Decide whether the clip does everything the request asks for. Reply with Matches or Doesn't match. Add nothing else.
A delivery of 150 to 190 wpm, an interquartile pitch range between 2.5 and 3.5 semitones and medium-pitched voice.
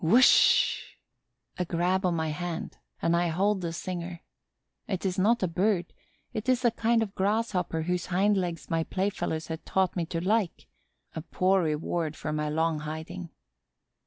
Matches